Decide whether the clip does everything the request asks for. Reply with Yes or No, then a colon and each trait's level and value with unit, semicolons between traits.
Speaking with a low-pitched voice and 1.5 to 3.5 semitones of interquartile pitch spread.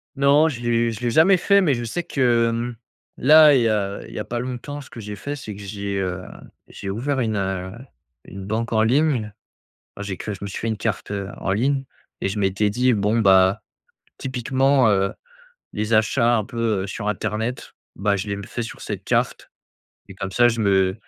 No: low, 110 Hz; average, 3.9 semitones